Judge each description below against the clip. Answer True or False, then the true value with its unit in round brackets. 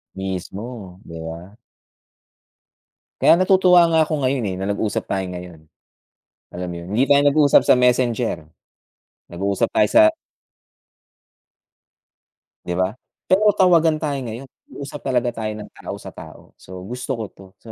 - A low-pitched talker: True (120 Hz)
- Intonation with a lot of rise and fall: True (7.0 semitones)